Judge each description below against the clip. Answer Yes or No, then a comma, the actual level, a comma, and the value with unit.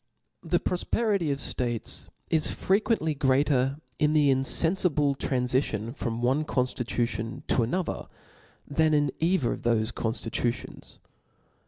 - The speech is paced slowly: Yes, slow, 115 wpm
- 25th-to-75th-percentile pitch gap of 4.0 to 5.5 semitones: Yes, average, 4.3 semitones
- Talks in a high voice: No, medium, 140 Hz